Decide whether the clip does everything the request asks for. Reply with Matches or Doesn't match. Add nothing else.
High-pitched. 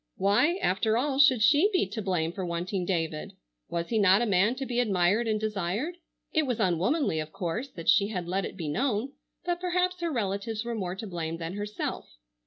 Matches